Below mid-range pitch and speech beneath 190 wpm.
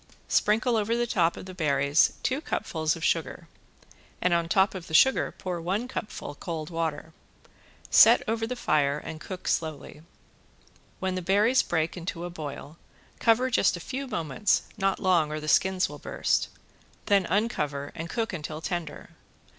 No: medium, 175 Hz; average, 165 wpm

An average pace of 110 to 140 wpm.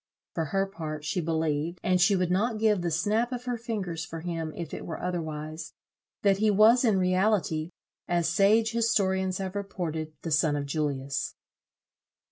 No: average, 170 wpm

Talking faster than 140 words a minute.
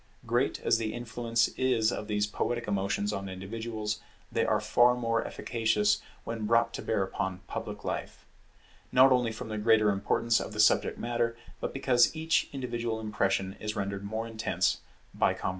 Yes: average, 170 wpm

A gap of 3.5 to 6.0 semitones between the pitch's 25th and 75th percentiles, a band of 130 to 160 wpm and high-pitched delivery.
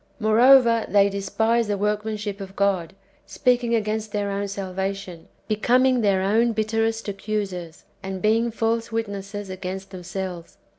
No: narrow, 2.5 semitones; slow, 135 wpm; high, 205 Hz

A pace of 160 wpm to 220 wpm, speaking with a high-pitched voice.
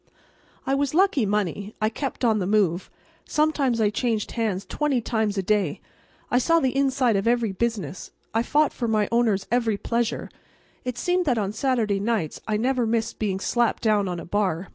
Yes: average, 185 wpm; high, 225 Hz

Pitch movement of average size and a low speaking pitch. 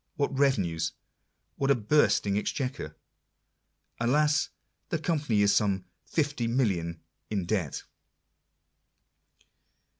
No: wide, 6.4 semitones; low, 115 Hz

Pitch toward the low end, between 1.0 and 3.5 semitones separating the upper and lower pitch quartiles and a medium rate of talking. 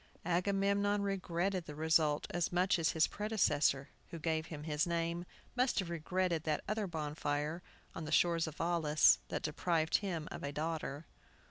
No: medium, 165 Hz; average, 2.9 semitones; average, 160 wpm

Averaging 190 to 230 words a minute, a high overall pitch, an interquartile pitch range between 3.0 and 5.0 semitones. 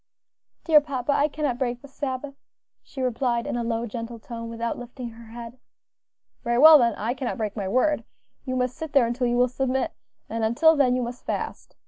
No: average, 200 wpm; high, 245 Hz; narrow, 2.6 semitones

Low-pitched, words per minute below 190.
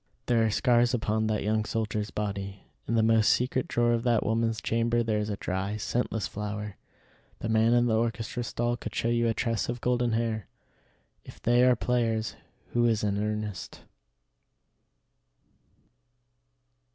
Yes: low, 115 Hz; average, 160 wpm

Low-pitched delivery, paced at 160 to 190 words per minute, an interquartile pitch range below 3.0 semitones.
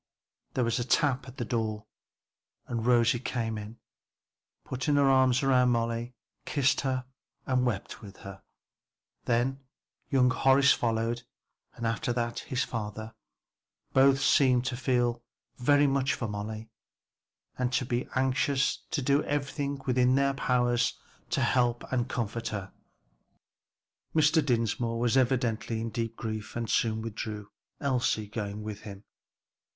No: low, 120 Hz; slow, 135 wpm; narrow, 2.6 semitones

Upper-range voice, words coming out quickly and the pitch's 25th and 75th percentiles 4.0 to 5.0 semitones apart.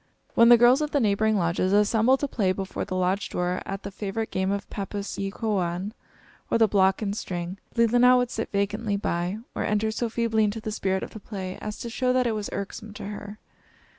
No: high, 205 Hz; fast, 220 wpm; average, 2.7 semitones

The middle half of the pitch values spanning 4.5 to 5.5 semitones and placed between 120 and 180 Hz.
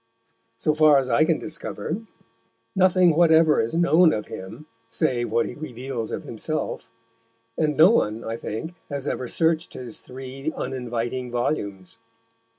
Yes: average, 5.2 semitones; low, 135 Hz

